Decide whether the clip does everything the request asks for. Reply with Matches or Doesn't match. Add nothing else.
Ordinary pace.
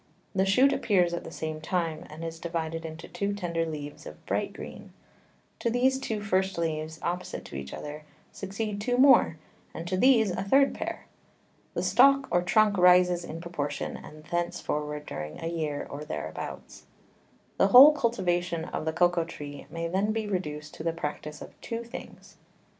Matches